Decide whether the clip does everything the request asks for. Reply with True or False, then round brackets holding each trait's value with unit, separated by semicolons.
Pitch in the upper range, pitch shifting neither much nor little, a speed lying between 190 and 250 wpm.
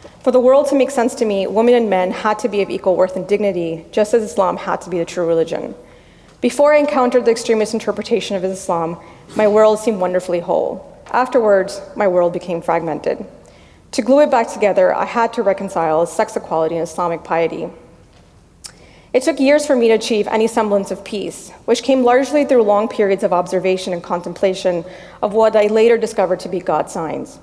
True (205 Hz; 4.2 semitones; 195 wpm)